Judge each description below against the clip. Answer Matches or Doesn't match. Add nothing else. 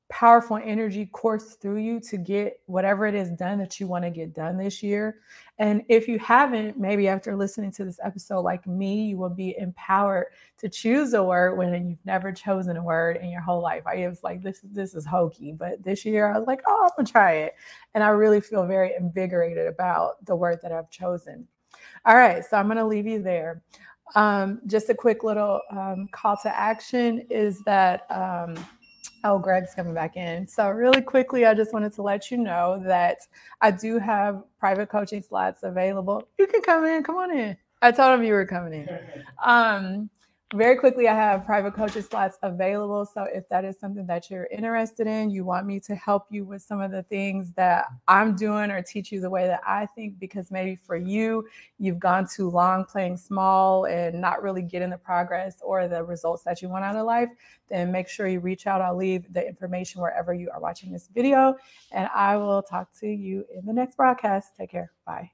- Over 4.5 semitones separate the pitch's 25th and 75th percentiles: Doesn't match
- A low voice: Doesn't match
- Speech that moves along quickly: Matches